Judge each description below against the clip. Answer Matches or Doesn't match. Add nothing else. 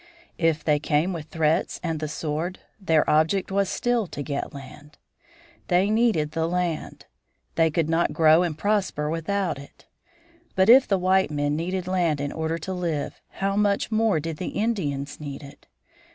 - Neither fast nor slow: Matches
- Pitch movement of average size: Matches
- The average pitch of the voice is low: Doesn't match